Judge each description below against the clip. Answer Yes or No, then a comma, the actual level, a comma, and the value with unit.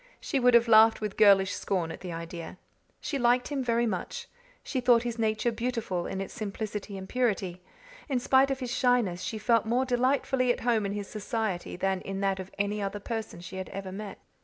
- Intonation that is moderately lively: Yes, average, 3.9 semitones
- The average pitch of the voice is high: Yes, high, 215 Hz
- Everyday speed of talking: No, fast, 210 wpm